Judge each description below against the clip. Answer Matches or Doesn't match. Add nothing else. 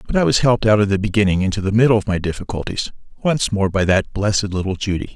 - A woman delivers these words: Doesn't match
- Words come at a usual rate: Doesn't match